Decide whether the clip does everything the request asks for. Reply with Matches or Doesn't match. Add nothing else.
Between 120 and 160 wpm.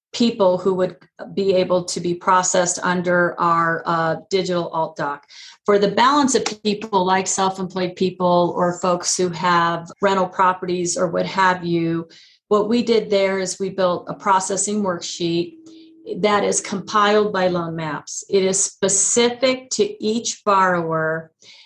Matches